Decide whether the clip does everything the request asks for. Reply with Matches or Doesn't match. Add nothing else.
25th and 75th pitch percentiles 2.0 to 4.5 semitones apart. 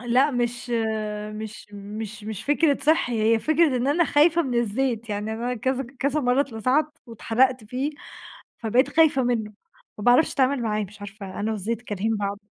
Matches